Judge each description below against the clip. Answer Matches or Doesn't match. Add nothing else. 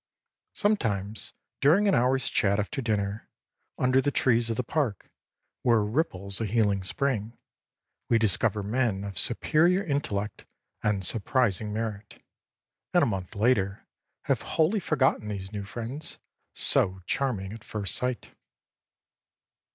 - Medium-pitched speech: Doesn't match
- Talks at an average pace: Doesn't match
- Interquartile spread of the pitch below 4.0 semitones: Doesn't match